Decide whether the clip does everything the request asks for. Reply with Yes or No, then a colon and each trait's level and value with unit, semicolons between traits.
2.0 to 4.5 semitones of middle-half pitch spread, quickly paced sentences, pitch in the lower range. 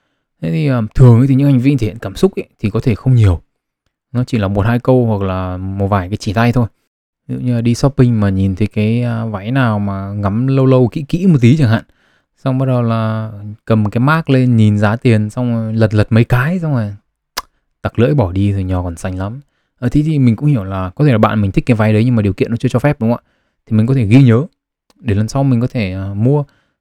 Yes: average, 3.8 semitones; fast, 265 wpm; low, 115 Hz